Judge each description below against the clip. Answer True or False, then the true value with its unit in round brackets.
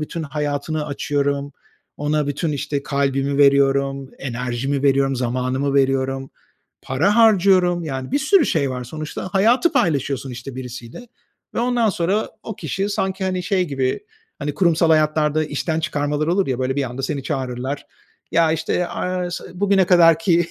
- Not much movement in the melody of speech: False (4.6 semitones)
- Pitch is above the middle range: False (145 Hz)